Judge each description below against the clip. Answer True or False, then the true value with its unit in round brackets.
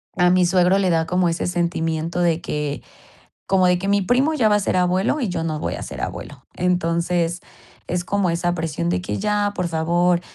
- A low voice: False (175 Hz)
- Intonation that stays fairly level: True (1.9 semitones)